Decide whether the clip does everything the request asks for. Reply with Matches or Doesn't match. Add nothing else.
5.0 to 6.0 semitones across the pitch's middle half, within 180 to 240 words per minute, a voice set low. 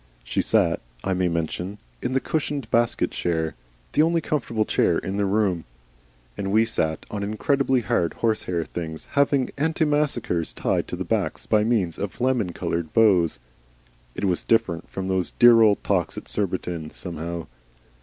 Doesn't match